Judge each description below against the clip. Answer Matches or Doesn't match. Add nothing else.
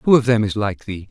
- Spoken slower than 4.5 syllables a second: Doesn't match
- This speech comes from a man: Matches